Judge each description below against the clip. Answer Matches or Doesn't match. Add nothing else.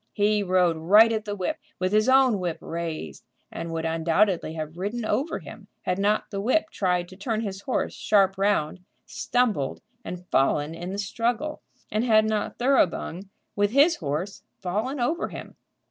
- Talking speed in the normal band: Matches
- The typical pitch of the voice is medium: Doesn't match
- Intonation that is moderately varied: Matches